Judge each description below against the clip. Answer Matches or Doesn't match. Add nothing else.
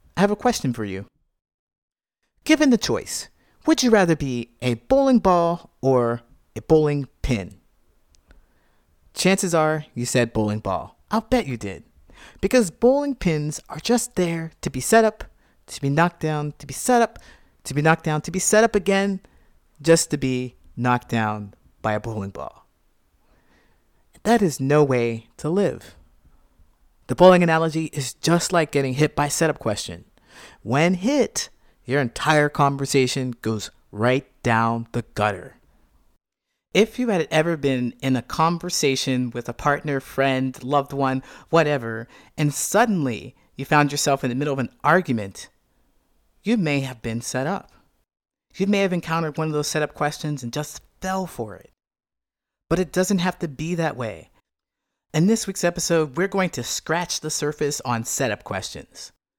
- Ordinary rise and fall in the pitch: Doesn't match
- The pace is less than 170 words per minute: Matches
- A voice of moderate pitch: Matches